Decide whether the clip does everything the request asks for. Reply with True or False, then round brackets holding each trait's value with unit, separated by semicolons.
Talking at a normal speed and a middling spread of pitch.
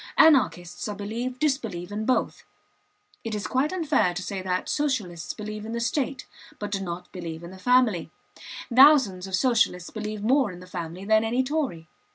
False (180 wpm; 5.8 semitones)